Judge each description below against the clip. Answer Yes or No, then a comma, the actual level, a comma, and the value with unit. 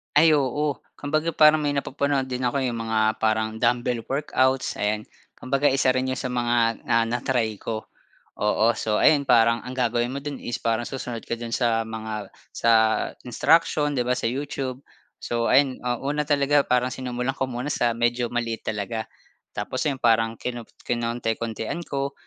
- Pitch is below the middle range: Yes, low, 125 Hz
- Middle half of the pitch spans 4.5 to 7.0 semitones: No, average, 3.0 semitones